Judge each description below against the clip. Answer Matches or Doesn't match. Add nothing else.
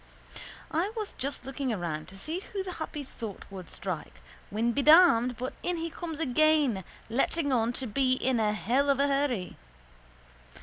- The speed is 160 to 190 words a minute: Matches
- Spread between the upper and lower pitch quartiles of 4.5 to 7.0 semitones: Matches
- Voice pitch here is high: Matches